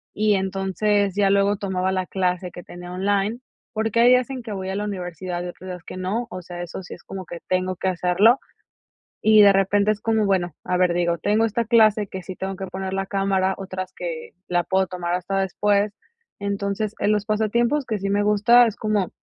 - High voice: Yes, high, 195 Hz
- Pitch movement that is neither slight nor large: No, narrow, 2.3 semitones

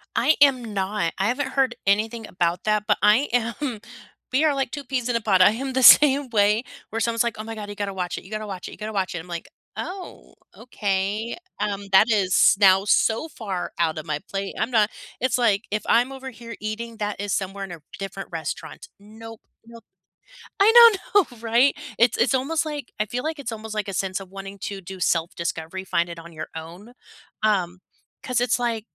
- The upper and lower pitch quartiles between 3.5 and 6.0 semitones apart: Yes, average, 4.0 semitones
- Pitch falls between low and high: No, high, 215 Hz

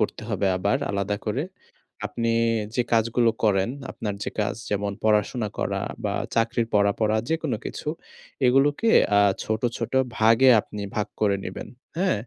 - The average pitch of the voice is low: Yes, low, 110 Hz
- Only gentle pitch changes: No, average, 3.1 semitones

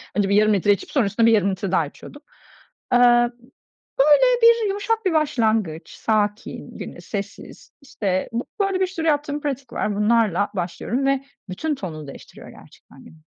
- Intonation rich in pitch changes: Yes, wide, 6.9 semitones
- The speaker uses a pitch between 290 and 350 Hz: No, high, 230 Hz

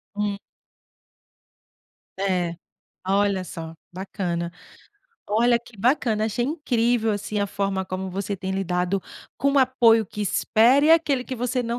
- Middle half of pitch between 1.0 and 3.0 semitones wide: No, average, 4.1 semitones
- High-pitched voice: Yes, high, 210 Hz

